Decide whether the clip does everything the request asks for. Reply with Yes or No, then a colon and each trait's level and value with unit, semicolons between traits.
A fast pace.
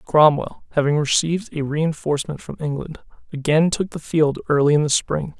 No: average, 165 wpm